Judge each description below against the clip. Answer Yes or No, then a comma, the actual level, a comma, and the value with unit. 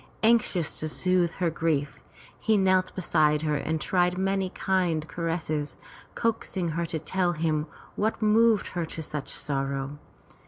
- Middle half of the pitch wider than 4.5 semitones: No, average, 3.5 semitones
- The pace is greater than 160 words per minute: No, average, 150 wpm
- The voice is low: No, medium, 170 Hz